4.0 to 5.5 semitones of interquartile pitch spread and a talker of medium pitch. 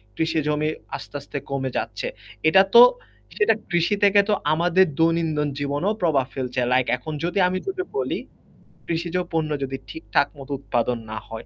Yes: average, 4.3 semitones; medium, 160 Hz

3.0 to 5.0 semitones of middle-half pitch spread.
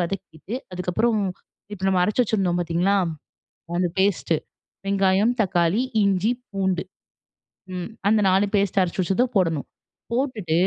No: narrow, 2.5 semitones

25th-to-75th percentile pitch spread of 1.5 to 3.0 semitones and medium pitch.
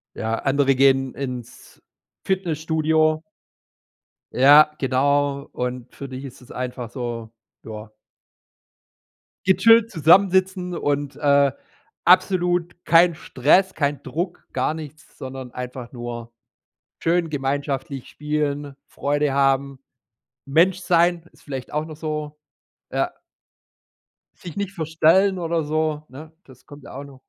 No: average, 3.7 semitones; medium, 145 Hz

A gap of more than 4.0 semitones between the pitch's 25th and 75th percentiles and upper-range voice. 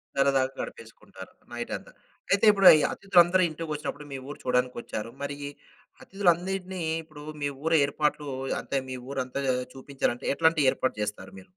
No: average, 4.7 semitones; medium, 145 Hz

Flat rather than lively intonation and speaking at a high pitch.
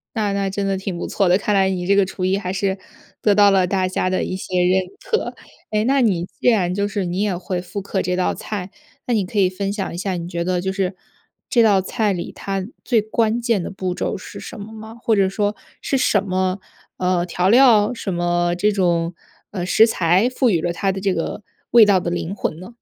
Yes: narrow, 2.3 semitones; high, 195 Hz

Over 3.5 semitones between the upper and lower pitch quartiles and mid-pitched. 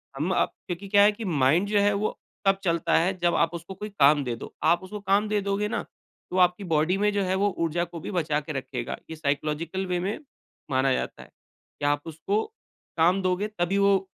Yes: average, 3.9 semitones; medium, 180 Hz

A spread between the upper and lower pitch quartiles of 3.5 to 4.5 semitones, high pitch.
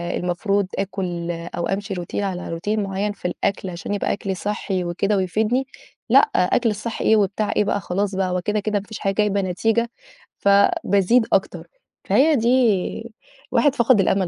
No: narrow, 2.5 semitones; high, 200 Hz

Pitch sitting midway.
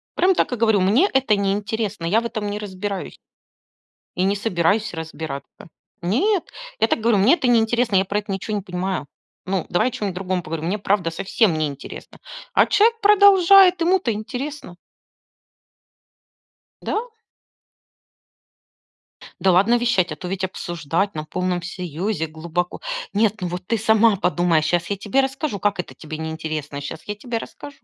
No: high, 200 Hz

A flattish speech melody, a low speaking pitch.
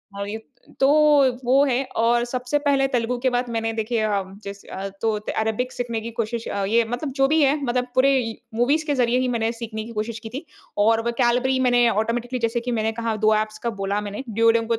No: narrow, 2.2 semitones; high, 235 Hz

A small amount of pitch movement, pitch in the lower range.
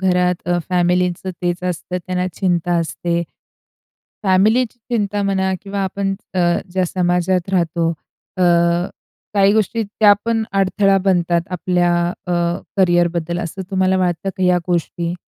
No: narrow, 1.9 semitones; medium, 180 Hz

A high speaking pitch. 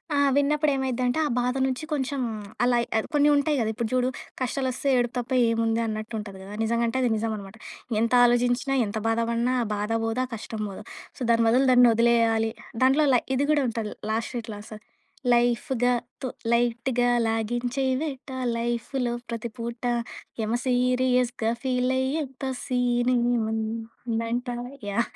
Yes: high, 240 Hz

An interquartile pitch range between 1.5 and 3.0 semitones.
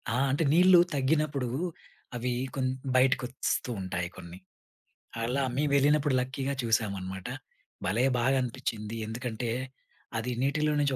No: average, 3.8 semitones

